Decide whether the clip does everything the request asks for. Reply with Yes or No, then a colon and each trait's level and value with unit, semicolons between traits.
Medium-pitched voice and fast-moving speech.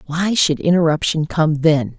No: medium, 160 Hz; average, 150 wpm